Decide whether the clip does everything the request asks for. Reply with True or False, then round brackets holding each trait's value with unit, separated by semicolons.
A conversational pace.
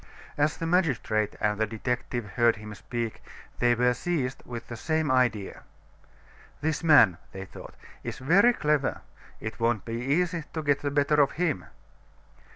True (160 wpm)